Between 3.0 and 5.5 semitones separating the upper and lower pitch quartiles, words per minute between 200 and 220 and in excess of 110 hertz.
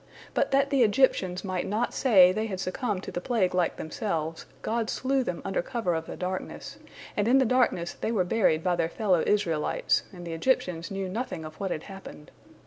Yes: average, 4.6 semitones; fast, 205 wpm; high, 190 Hz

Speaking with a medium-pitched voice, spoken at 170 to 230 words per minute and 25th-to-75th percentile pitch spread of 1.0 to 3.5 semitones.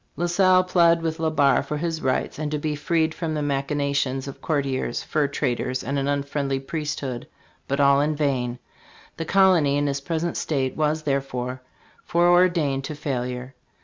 Yes: medium, 145 Hz; average, 175 wpm; average, 2.8 semitones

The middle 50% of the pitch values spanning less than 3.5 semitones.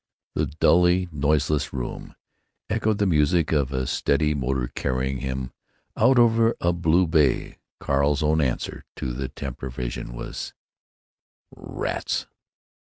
No: average, 4.7 semitones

